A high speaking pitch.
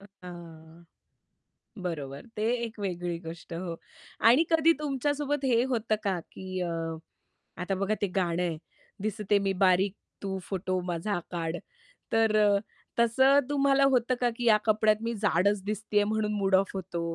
Yes: high, 200 Hz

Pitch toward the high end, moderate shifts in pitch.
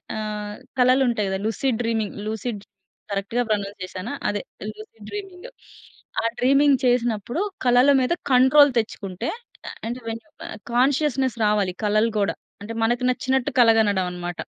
Yes: high, 230 Hz; average, 3.5 semitones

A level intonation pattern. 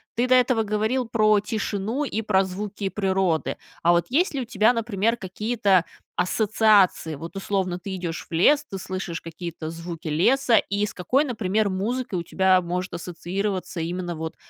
No: average, 3.8 semitones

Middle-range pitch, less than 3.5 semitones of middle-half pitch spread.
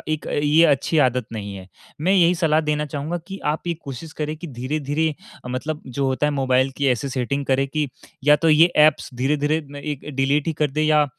Yes: medium, 150 Hz; narrow, 2.6 semitones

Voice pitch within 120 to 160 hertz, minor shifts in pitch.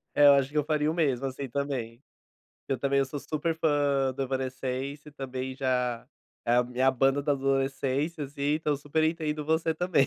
Yes: medium, 140 Hz; narrow, 2.2 semitones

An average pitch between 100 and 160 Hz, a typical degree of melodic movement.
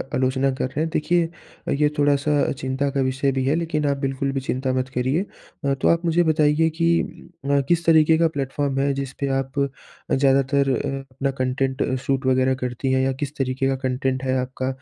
No: low, 135 Hz; narrow, 1.9 semitones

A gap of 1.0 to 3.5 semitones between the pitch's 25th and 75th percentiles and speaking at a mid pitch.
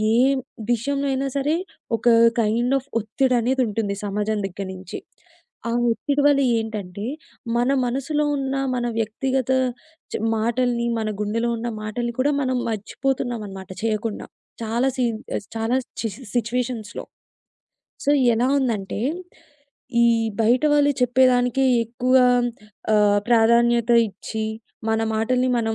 No: average, 2.9 semitones; high, 235 Hz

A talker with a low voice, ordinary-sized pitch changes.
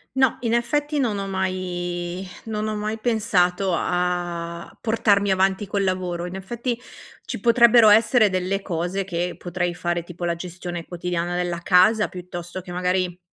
No: medium, 185 Hz; average, 3.2 semitones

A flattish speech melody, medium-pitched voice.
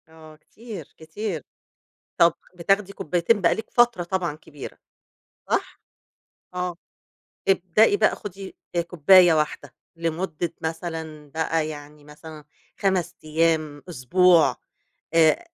No: average, 3.3 semitones; medium, 165 Hz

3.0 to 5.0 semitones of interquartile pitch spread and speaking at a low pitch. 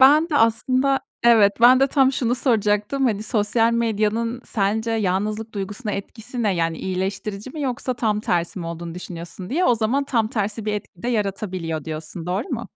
No: average, 3.7 semitones; high, 215 Hz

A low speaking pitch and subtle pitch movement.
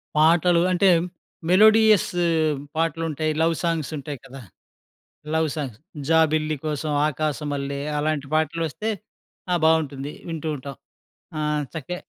No: medium, 155 Hz; narrow, 2.1 semitones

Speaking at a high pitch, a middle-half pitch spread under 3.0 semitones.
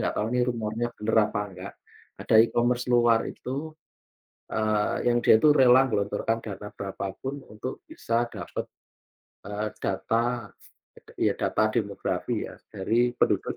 No: low, 115 Hz; narrow, 2.6 semitones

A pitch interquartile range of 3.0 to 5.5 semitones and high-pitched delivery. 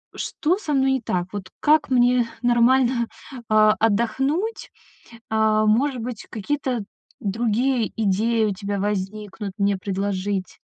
Yes: average, 4.1 semitones; high, 225 Hz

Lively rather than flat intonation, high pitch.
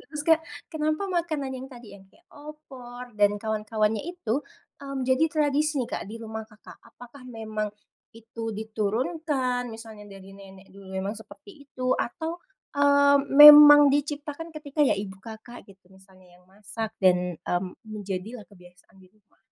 Yes: wide, 5.9 semitones; high, 225 Hz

